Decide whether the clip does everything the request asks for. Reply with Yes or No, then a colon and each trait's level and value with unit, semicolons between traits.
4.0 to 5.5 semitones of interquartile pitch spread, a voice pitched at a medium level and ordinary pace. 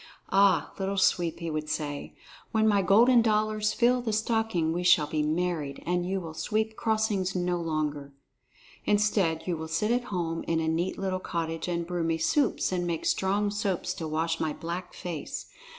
Yes: average, 4.4 semitones; medium, 180 Hz; average, 180 wpm